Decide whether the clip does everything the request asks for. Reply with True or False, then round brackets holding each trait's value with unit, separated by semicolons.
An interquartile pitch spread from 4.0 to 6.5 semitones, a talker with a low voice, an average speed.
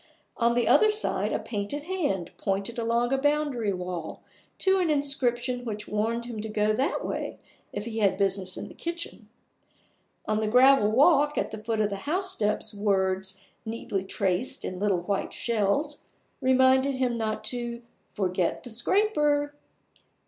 False (5.2 semitones; 235 Hz; 155 wpm)